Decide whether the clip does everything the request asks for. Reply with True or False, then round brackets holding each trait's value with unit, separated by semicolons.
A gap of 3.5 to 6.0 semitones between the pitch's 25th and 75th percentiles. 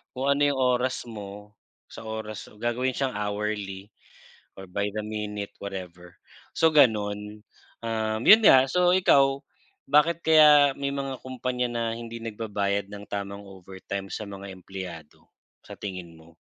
True (4.6 semitones)